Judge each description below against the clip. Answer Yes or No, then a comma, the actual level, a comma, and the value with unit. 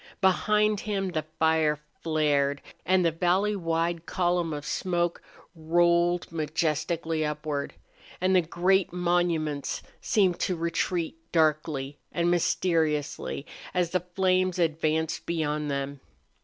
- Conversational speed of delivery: No, slow, 115 wpm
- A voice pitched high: No, medium, 165 Hz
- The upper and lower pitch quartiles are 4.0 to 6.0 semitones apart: No, narrow, 2.5 semitones